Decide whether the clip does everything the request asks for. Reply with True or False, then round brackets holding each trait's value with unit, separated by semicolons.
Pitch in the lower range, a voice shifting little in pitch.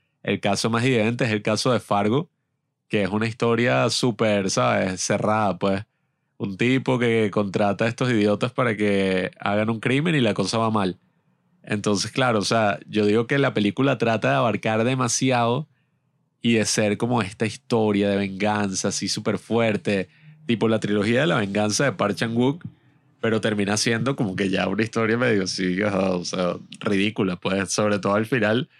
False (110 Hz; 3.9 semitones)